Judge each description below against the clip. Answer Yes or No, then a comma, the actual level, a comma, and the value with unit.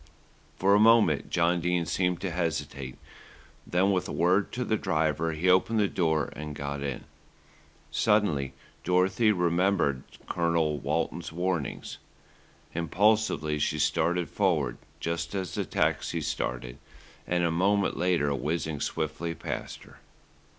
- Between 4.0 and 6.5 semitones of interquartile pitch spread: No, average, 3.6 semitones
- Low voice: Yes, very low, 85 Hz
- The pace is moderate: No, slow, 130 wpm